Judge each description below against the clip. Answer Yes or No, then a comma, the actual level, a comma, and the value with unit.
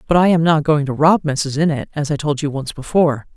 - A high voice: No, medium, 150 Hz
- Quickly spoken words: Yes, fast, 270 wpm